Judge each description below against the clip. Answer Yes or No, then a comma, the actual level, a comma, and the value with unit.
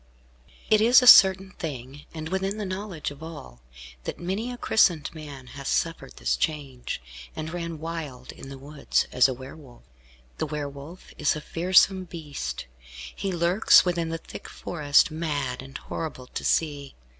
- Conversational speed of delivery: Yes, average, 165 wpm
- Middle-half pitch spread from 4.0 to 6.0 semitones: Yes, average, 4.3 semitones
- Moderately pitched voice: Yes, medium, 155 Hz